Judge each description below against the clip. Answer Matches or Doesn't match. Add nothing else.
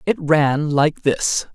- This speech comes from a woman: Doesn't match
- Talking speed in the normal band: Matches